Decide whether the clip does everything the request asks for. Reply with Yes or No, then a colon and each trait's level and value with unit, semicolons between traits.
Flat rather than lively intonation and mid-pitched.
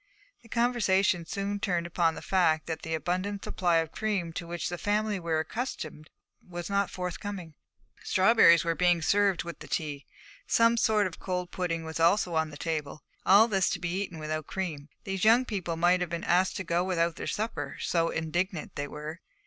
No: average, 3.3 semitones; medium, 175 Hz